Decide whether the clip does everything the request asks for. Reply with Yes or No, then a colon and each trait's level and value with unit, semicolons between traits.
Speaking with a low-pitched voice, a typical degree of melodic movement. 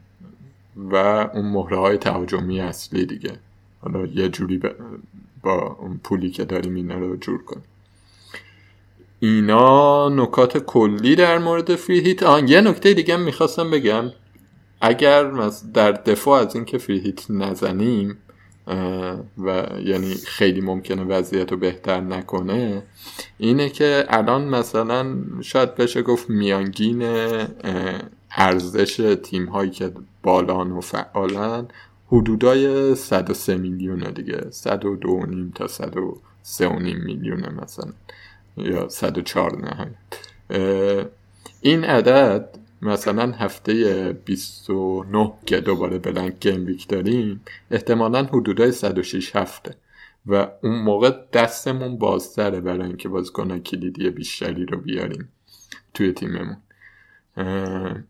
Yes: low, 100 Hz; average, 4.1 semitones